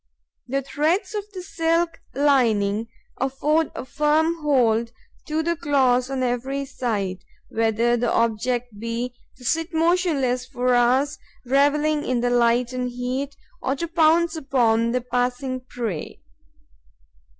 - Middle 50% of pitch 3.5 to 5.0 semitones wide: Yes, average, 3.9 semitones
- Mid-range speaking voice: No, very high, 255 Hz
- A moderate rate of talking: No, slow, 130 wpm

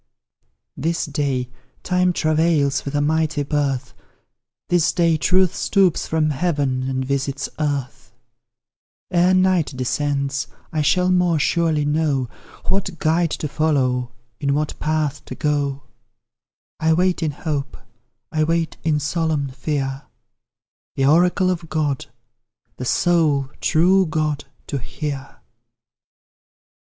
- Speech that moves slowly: Yes, slow, 120 wpm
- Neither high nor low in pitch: Yes, medium, 150 Hz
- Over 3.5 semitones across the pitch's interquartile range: No, average, 3.1 semitones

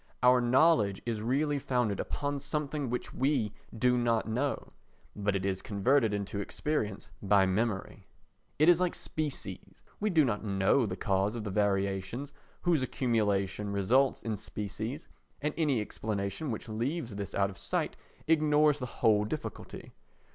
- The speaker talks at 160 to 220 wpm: No, average, 145 wpm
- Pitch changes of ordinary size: No, wide, 5.8 semitones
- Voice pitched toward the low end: Yes, low, 115 Hz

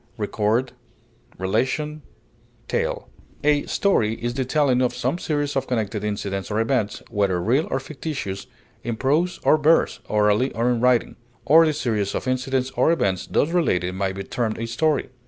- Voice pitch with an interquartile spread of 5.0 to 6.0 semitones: Yes, wide, 5.5 semitones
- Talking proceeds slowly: No, average, 160 wpm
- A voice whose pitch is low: Yes, low, 125 Hz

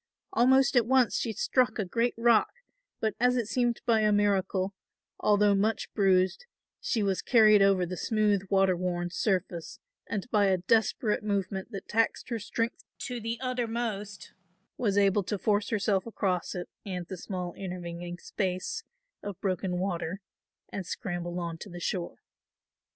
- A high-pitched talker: Yes, high, 200 Hz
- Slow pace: No, average, 155 wpm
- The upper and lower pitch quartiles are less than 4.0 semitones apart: Yes, average, 3.5 semitones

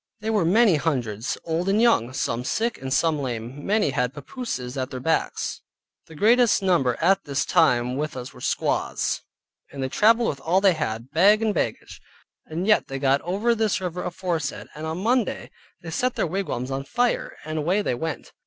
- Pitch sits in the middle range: Yes, medium, 160 Hz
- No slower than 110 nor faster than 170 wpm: No, average, 190 wpm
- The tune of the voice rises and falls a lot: Yes, wide, 7.3 semitones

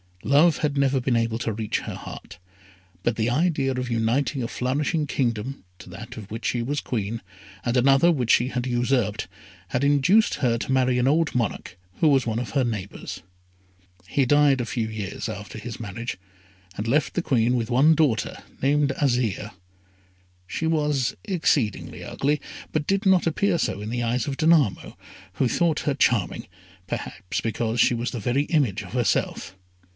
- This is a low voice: Yes, low, 125 Hz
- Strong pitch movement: No, average, 4.0 semitones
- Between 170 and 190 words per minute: Yes, average, 175 wpm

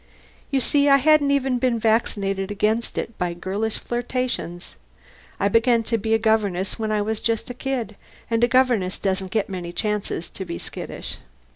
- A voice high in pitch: Yes, high, 220 Hz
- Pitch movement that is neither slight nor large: Yes, average, 3.8 semitones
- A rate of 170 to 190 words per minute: Yes, average, 180 wpm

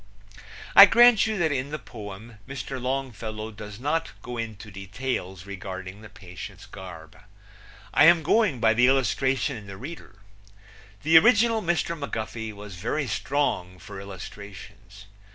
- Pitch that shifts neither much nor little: No, wide, 6.6 semitones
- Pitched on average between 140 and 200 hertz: No, low, 115 Hz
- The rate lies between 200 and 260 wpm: No, average, 140 wpm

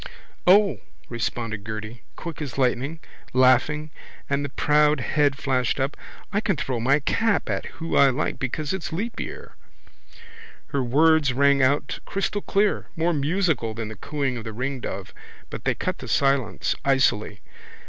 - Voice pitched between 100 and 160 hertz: Yes, medium, 140 Hz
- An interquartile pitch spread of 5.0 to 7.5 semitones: No, average, 3.9 semitones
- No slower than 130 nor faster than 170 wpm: Yes, average, 150 wpm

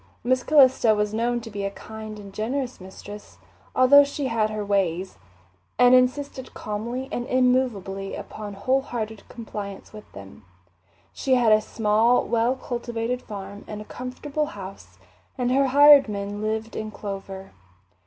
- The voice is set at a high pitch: Yes, high, 220 Hz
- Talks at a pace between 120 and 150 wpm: Yes, average, 145 wpm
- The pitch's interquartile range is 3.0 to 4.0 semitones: Yes, average, 3.6 semitones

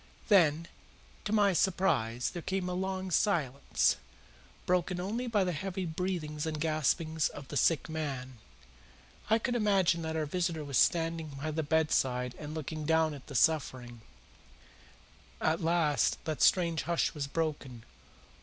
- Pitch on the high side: No, medium, 160 Hz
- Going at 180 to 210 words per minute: No, average, 145 wpm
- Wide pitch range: No, average, 3.6 semitones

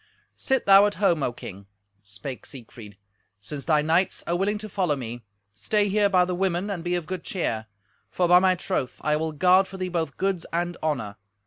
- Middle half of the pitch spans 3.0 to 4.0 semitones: No, wide, 5.5 semitones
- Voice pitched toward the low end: No, medium, 175 Hz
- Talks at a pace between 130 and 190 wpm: No, fast, 205 wpm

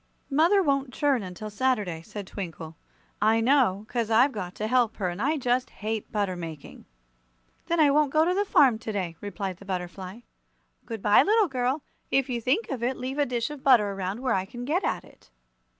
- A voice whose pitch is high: Yes, high, 235 Hz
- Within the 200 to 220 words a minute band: Yes, fast, 205 wpm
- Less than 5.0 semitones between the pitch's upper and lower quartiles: No, wide, 5.5 semitones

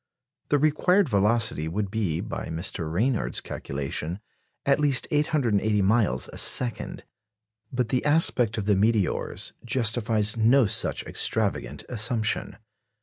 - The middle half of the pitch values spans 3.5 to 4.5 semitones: Yes, average, 4.2 semitones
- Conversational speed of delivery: No, slow, 120 wpm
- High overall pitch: No, low, 110 Hz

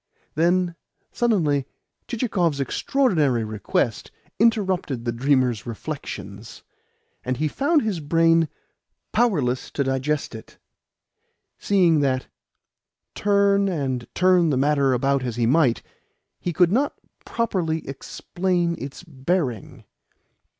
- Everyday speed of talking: No, slow, 105 wpm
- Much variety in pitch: Yes, wide, 6.0 semitones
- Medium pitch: Yes, medium, 155 Hz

